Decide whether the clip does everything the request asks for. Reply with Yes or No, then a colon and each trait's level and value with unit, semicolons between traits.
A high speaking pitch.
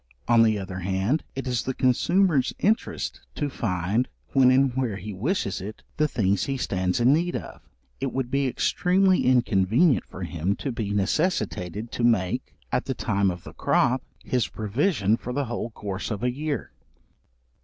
No: low, 120 Hz